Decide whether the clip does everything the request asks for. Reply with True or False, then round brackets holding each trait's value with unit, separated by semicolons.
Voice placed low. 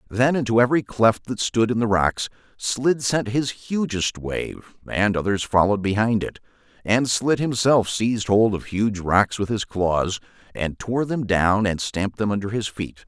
True (110 Hz)